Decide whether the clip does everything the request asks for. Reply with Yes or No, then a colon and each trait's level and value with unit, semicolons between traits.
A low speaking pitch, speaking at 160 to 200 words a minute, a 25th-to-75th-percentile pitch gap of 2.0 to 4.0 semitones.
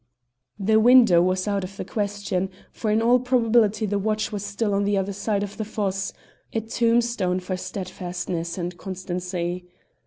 No: high, 200 Hz; average, 165 wpm; average, 2.9 semitones